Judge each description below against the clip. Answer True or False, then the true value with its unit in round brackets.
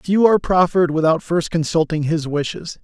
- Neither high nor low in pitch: True (165 Hz)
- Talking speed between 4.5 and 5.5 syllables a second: True (5.4 syllables/s)